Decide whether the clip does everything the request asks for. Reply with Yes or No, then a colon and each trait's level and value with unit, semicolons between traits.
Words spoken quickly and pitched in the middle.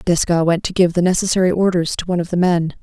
Yes: fast, 255 wpm; medium, 175 Hz